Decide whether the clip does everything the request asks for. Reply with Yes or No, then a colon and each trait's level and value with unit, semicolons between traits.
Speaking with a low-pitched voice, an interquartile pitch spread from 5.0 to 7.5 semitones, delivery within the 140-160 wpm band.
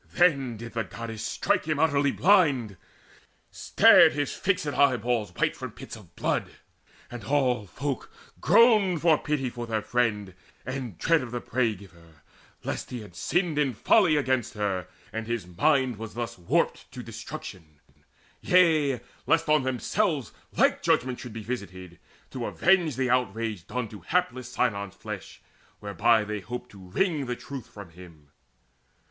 Yes: low, 125 Hz; wide, 5.6 semitones; average, 155 wpm